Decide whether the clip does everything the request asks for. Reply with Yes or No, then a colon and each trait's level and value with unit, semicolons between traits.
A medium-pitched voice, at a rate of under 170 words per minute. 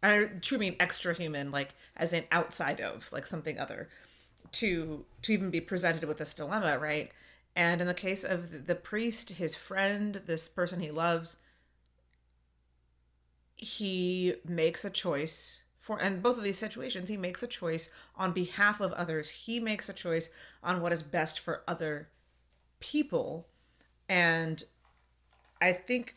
Yes: medium, 175 Hz; average, 155 wpm